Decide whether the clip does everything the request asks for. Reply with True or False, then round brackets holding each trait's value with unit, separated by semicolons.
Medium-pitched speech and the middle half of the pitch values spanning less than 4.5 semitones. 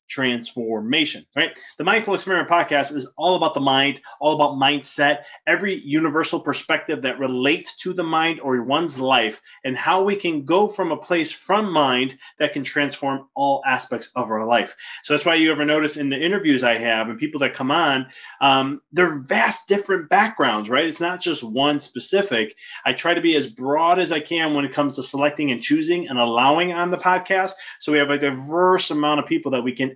True (150 Hz; 3.9 semitones)